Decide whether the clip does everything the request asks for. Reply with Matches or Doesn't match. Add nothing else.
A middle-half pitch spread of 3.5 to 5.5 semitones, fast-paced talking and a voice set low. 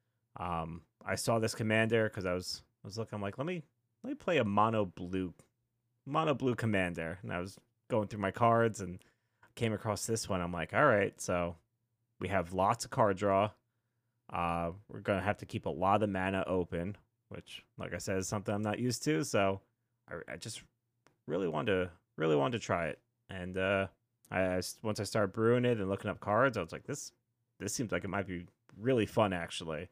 Matches